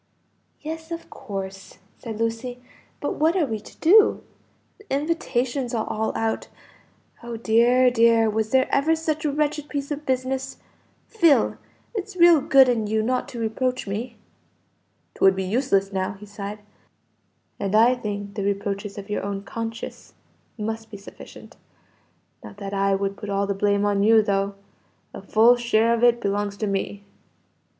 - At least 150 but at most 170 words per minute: Yes, average, 160 wpm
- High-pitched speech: Yes, high, 225 Hz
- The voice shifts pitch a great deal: No, average, 4.5 semitones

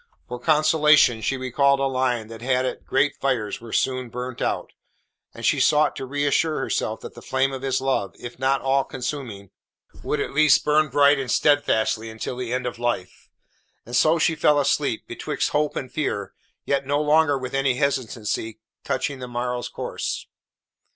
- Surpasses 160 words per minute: Yes, average, 180 wpm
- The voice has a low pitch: Yes, low, 130 Hz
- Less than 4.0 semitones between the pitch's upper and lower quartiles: Yes, average, 2.7 semitones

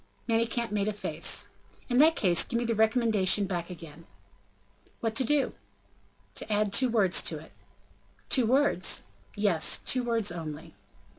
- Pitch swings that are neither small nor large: Yes, average, 4.3 semitones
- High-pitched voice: Yes, high, 215 Hz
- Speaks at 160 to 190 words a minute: No, average, 150 wpm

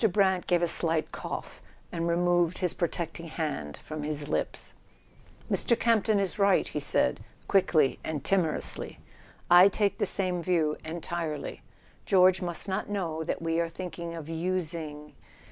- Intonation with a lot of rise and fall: No, narrow, 2.6 semitones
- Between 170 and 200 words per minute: No, average, 150 wpm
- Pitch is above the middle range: No, medium, 170 Hz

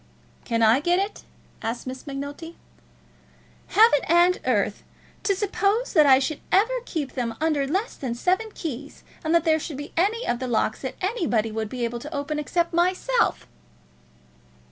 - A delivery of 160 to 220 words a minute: Yes, average, 165 wpm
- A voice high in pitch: Yes, very high, 310 Hz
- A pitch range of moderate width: No, wide, 6.0 semitones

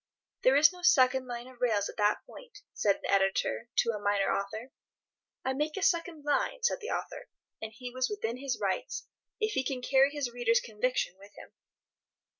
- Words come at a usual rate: Yes, average, 195 wpm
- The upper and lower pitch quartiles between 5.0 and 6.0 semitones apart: Yes, wide, 5.4 semitones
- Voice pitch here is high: Yes, very high, 255 Hz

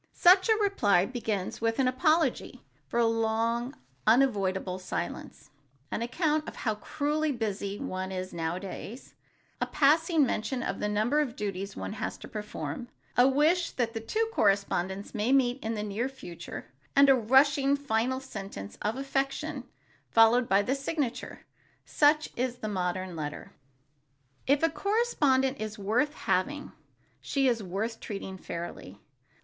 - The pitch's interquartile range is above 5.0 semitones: Yes, wide, 5.6 semitones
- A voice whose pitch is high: Yes, high, 235 Hz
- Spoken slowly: No, average, 150 wpm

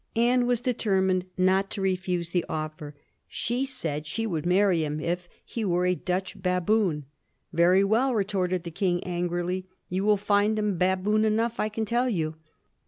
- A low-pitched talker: No, medium, 185 Hz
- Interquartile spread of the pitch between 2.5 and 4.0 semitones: Yes, average, 3.4 semitones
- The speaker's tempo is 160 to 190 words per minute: Yes, average, 175 wpm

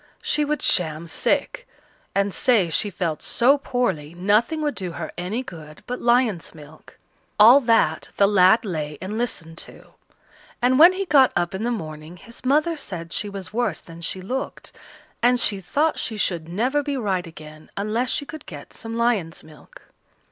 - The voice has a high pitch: Yes, high, 205 Hz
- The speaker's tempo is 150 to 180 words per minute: Yes, average, 175 wpm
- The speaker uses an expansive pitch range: Yes, wide, 6.6 semitones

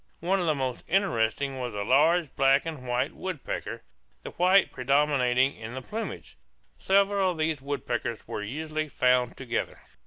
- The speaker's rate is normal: Yes, average, 155 wpm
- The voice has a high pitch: No, medium, 140 Hz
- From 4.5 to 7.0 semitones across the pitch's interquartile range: Yes, average, 5.1 semitones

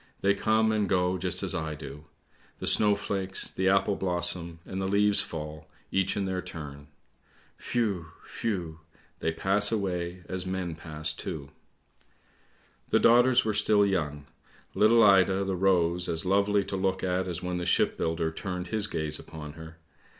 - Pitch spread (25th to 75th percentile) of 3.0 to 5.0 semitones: Yes, average, 3.3 semitones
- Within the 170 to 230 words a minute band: No, average, 160 wpm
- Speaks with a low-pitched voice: Yes, very low, 95 Hz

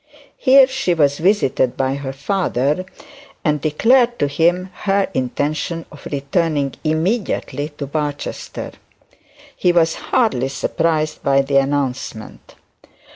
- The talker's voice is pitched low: No, medium, 155 Hz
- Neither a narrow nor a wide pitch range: Yes, average, 4.7 semitones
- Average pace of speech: No, slow, 115 wpm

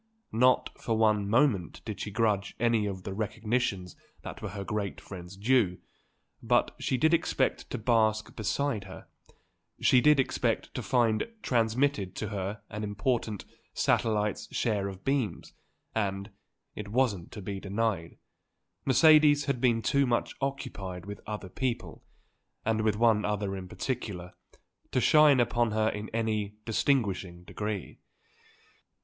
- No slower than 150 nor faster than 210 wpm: No, average, 140 wpm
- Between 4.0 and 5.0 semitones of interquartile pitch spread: No, average, 3.4 semitones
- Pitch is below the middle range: Yes, low, 110 Hz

